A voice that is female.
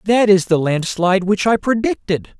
No: male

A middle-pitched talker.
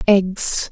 No: high, 195 Hz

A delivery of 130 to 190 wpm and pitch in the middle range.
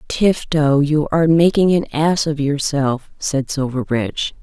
Yes: slow, 135 wpm; medium, 150 Hz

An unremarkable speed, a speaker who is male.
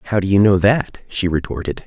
No: fast, 225 wpm; male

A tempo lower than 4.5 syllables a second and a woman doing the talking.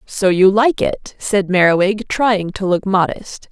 Yes: 3.9 syllables/s; female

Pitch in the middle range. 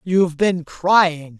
Yes: medium, 170 Hz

